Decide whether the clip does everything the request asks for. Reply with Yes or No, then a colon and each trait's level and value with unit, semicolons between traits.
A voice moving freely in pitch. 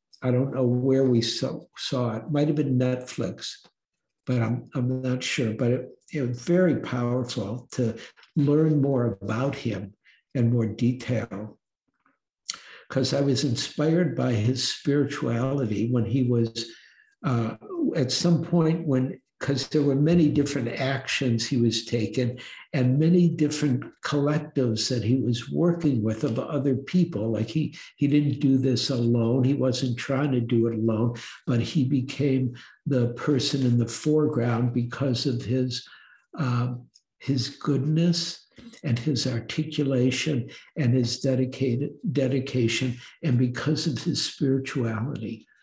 No: average, 3.2 semitones